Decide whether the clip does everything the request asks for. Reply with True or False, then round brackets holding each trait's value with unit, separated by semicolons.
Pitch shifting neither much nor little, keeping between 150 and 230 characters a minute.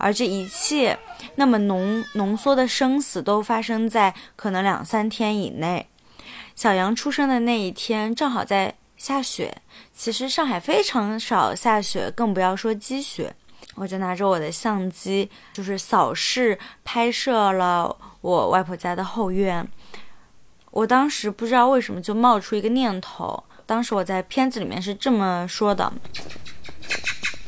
True (3.8 semitones; 225 characters per minute)